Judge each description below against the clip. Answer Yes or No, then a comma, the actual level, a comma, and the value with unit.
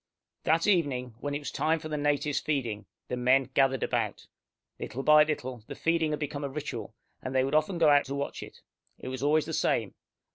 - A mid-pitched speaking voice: Yes, medium, 145 Hz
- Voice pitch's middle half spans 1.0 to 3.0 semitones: Yes, average, 2.7 semitones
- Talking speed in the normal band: No, fast, 215 wpm